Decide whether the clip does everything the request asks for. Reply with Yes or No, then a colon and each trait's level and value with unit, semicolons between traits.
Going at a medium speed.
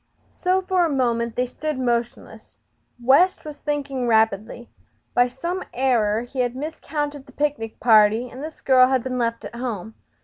Yes: average, 165 wpm